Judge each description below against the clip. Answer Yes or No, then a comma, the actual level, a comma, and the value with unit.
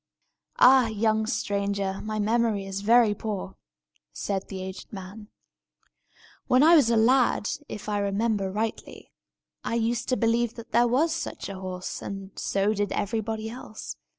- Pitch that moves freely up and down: No, average, 2.8 semitones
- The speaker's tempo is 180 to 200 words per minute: No, average, 150 wpm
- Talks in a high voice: Yes, high, 215 Hz